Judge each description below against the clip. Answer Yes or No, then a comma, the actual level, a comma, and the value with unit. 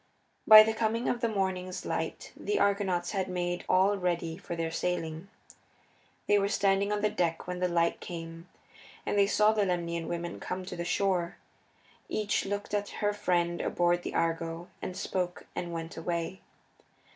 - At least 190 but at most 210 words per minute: No, average, 170 wpm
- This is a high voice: No, medium, 180 Hz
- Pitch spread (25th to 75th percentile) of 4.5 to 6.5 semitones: No, average, 2.8 semitones